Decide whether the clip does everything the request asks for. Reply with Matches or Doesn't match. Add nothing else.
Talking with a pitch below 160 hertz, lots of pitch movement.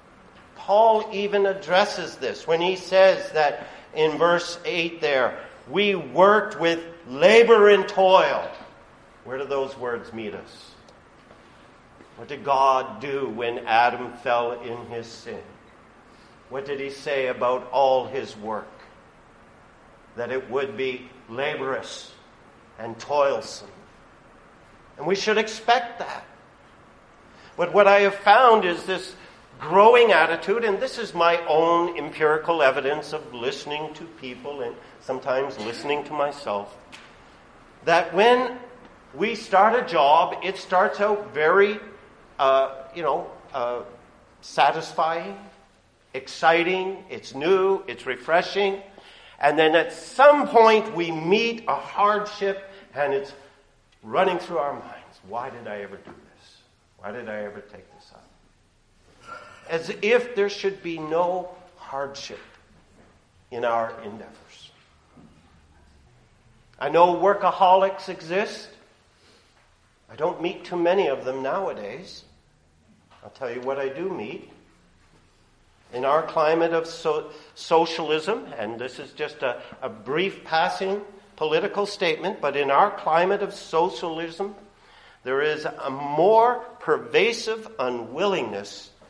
Doesn't match